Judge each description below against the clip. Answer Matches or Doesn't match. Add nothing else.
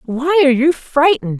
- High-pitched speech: Matches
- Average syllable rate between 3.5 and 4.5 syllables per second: Doesn't match